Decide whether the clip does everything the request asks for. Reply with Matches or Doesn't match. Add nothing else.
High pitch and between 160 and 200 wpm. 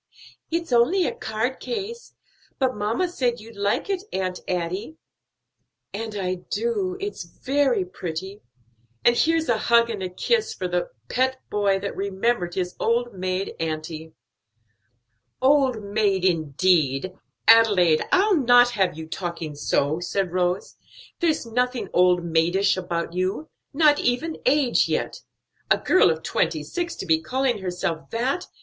Doesn't match